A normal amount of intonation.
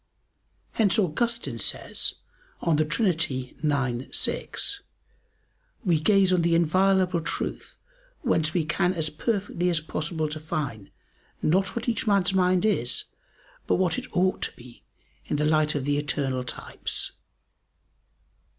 Yes: average, 4.1 semitones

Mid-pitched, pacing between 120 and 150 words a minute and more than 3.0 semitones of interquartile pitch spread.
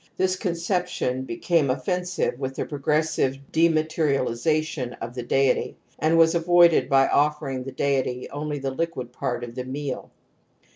Yes: medium, 145 Hz; average, 145 wpm; average, 4.0 semitones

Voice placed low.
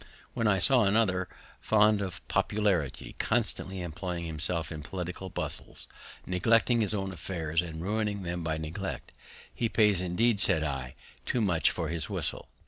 Yes: very low, 90 Hz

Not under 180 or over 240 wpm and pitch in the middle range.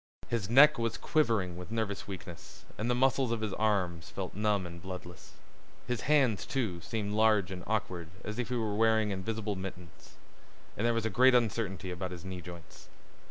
No: average, 185 wpm; low, 105 Hz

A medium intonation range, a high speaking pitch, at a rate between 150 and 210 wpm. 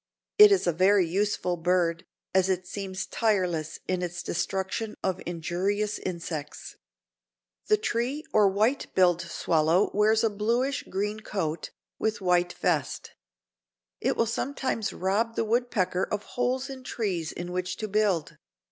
No: average, 3.7 semitones; high, 195 Hz; average, 140 wpm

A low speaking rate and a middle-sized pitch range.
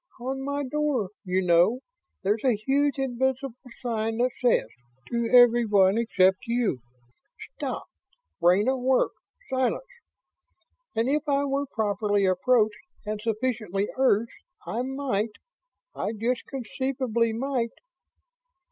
Yes: slow, 115 wpm; average, 3.9 semitones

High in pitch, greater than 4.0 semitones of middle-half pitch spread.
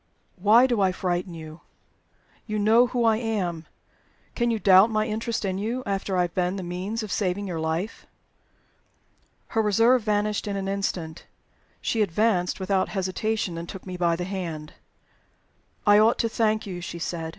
No: high, 195 Hz; average, 3.5 semitones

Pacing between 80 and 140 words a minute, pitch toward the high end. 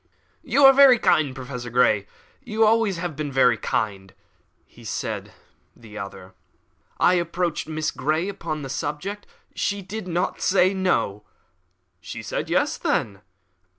No: slow, 135 wpm; medium, 155 Hz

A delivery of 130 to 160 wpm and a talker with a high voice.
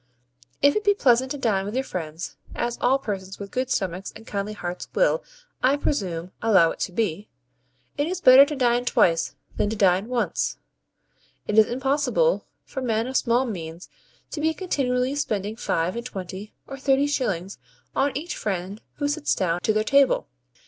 No: average, 180 wpm; high, 235 Hz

